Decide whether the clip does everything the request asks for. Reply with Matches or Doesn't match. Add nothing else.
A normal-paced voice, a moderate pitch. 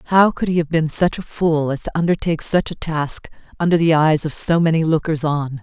Doesn't match